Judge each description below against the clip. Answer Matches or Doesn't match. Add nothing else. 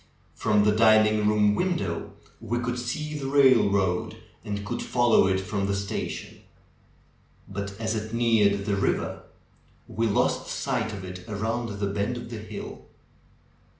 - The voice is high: Doesn't match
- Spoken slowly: Doesn't match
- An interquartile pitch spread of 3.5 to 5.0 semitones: Doesn't match